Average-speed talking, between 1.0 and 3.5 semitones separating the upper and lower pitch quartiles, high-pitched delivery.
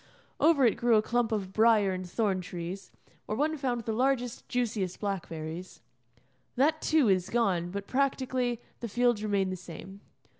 No: average, 160 wpm; average, 4.6 semitones; high, 215 Hz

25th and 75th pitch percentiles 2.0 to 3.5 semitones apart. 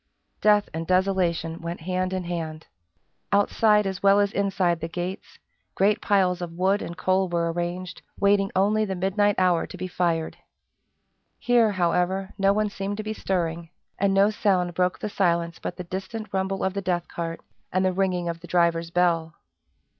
Yes: narrow, 2.4 semitones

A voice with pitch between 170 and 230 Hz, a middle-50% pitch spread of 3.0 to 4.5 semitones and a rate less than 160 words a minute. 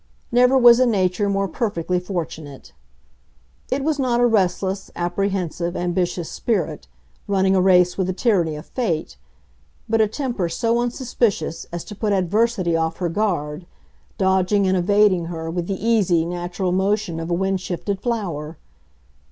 Yes: high, 190 Hz; average, 3.7 semitones; average, 150 wpm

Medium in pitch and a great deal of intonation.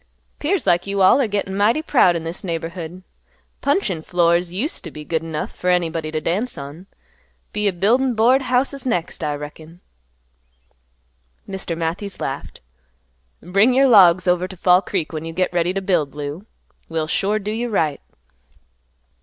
No: medium, 180 Hz; average, 4.2 semitones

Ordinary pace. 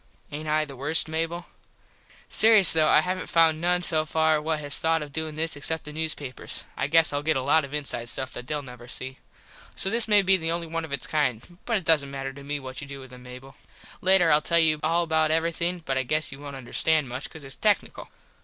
No: fast, 240 wpm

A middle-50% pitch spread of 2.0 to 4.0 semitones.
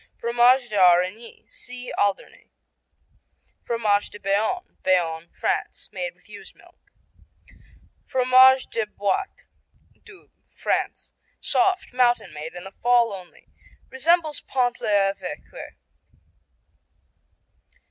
No: average, 4.8 semitones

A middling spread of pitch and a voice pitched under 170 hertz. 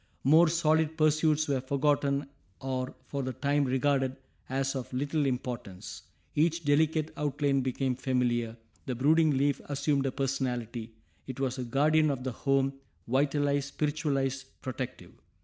No: narrow, 2.2 semitones; low, 135 Hz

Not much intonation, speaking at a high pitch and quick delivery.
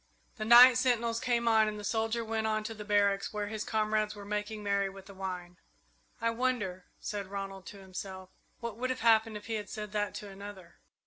Yes: narrow, 2.1 semitones; high, 210 Hz; fast, 215 wpm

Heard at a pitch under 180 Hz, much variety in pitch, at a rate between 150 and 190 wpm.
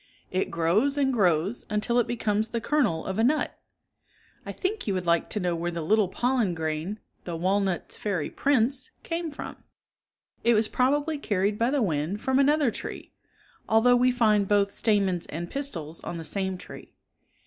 No: high, 210 Hz; wide, 6.0 semitones; average, 180 wpm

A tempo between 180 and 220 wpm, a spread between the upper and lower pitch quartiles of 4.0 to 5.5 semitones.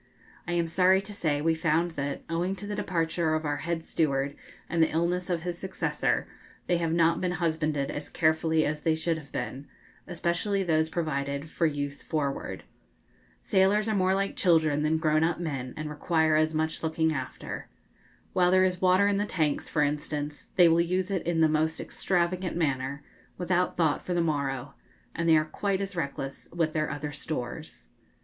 No: average, 185 wpm; average, 2.7 semitones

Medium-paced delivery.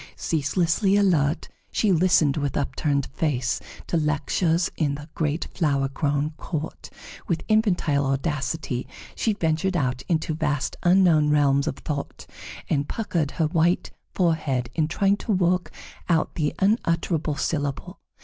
No: slow, 130 wpm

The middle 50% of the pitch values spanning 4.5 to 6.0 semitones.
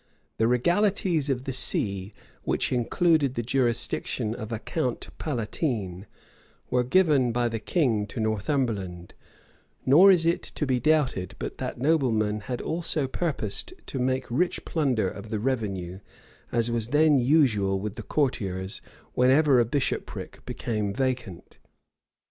Yes: average, 5.3 semitones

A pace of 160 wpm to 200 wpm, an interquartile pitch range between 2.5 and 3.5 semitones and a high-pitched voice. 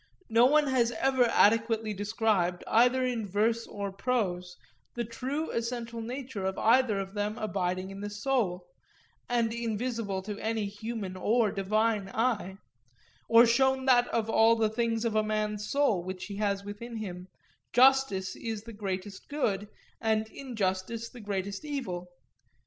No: average, 150 wpm; average, 3.0 semitones; high, 220 Hz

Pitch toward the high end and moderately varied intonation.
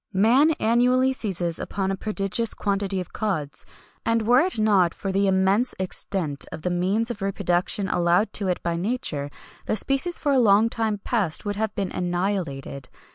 Yes: high, 200 Hz; average, 4.0 semitones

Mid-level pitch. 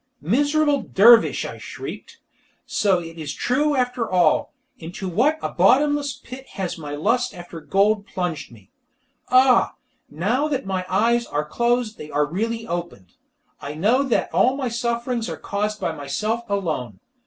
No: high, 215 Hz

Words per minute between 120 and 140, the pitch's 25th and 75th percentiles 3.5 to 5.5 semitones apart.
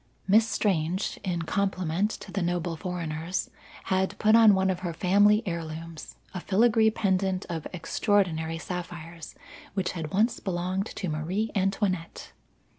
No: slow, 135 wpm; average, 3.1 semitones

